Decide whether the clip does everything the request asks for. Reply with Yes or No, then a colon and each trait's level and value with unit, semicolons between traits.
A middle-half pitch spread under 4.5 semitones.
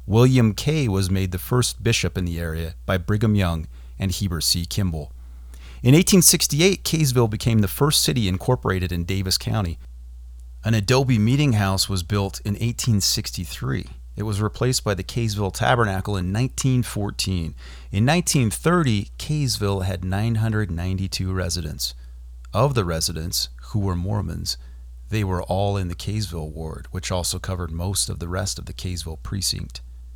No: average, 5.0 semitones